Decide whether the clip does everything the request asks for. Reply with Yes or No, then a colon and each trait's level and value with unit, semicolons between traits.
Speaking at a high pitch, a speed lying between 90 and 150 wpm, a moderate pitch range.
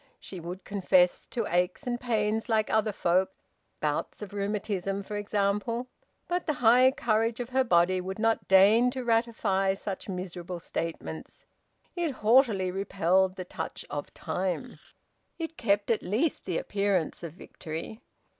Yes: high, 200 Hz; average, 145 wpm; average, 3.8 semitones